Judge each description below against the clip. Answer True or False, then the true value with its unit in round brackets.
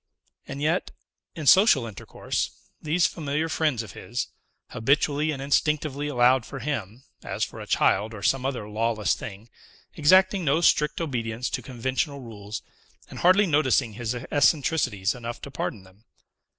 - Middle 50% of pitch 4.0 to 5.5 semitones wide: True (4.9 semitones)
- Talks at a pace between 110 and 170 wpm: True (150 wpm)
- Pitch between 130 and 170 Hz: True (135 Hz)